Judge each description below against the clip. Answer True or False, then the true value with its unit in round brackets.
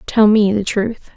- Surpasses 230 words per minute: False (205 wpm)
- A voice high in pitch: True (210 Hz)